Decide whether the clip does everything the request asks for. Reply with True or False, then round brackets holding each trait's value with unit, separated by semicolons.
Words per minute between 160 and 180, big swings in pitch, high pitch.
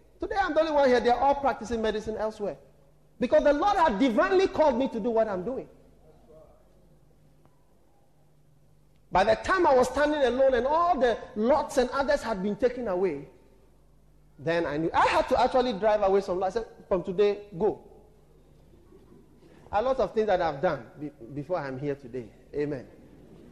True (175 wpm; 7.1 semitones; 230 Hz)